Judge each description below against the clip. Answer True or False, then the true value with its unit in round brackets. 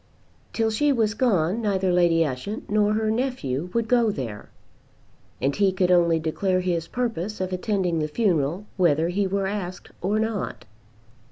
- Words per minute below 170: True (160 wpm)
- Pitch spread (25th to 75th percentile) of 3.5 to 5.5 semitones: True (4.2 semitones)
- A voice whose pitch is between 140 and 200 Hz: True (190 Hz)